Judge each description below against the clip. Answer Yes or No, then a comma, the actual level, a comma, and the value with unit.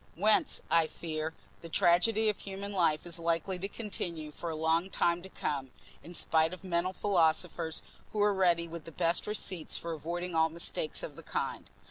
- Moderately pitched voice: Yes, medium, 170 Hz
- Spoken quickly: No, average, 185 wpm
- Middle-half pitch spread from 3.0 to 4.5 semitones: No, narrow, 2.6 semitones